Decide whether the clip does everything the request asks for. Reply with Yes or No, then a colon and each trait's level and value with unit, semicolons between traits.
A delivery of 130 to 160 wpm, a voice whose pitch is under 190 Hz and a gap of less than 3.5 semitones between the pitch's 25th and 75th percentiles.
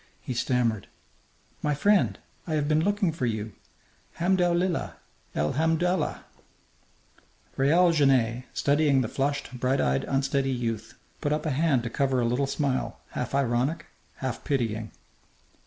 No: average, 140 wpm; low, 135 Hz; average, 4.3 semitones